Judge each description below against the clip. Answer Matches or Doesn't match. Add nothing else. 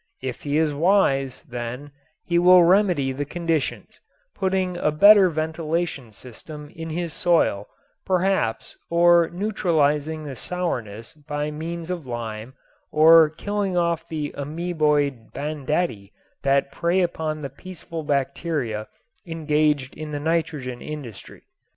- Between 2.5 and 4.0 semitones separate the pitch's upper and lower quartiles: Matches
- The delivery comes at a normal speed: Doesn't match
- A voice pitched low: Doesn't match